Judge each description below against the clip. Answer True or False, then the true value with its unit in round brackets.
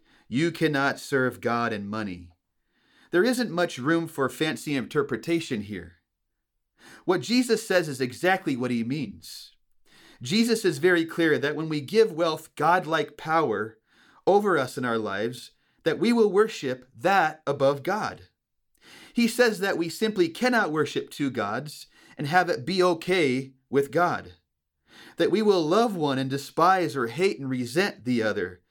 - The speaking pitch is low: False (155 Hz)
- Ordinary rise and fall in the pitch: False (6.1 semitones)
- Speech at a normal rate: True (155 wpm)